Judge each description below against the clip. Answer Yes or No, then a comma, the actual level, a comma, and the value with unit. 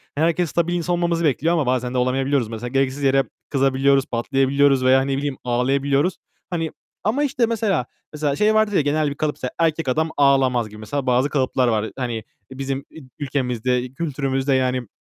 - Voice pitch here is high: No, low, 135 Hz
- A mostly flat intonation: No, average, 3.4 semitones